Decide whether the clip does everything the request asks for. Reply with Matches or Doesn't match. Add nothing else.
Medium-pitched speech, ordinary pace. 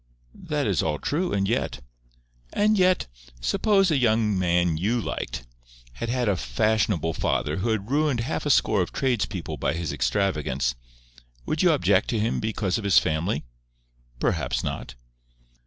Doesn't match